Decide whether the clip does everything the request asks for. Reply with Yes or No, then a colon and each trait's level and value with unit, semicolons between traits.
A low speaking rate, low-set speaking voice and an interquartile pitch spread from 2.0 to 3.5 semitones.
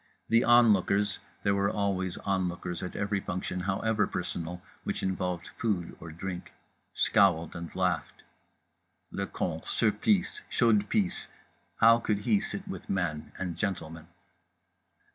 Yes: slow, 125 wpm; very low, 95 Hz; average, 3.1 semitones